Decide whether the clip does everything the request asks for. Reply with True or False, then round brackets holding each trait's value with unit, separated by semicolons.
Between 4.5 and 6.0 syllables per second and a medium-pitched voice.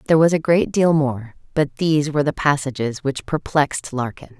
True (5.6 syllables/s; 145 Hz)